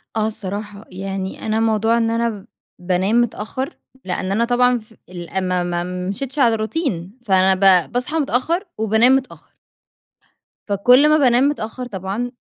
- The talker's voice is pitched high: Yes, high, 220 Hz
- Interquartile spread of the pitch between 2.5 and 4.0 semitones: No, average, 4.4 semitones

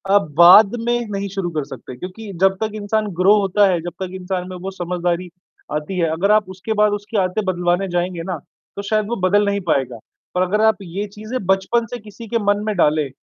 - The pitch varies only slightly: No, average, 3.0 semitones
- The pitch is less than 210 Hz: Yes, high, 190 Hz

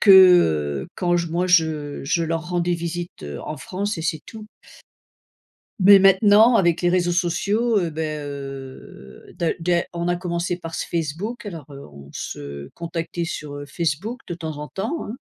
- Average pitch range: Yes, average, 3.2 semitones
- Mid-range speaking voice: Yes, medium, 170 Hz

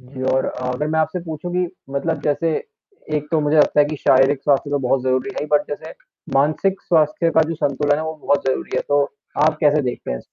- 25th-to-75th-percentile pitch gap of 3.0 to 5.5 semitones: No, narrow, 2.6 semitones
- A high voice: No, medium, 150 Hz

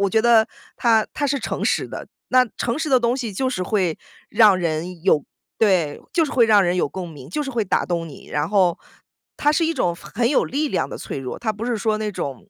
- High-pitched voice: Yes, high, 215 Hz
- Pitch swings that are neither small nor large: No, wide, 5.7 semitones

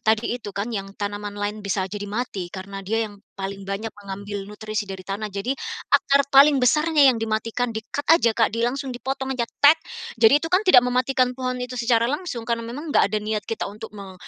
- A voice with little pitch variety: No, average, 3.7 semitones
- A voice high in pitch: Yes, high, 225 Hz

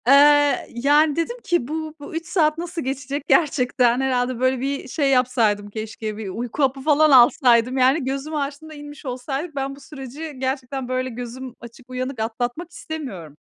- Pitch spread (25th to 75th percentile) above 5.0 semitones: No, average, 3.1 semitones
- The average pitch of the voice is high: Yes, very high, 265 Hz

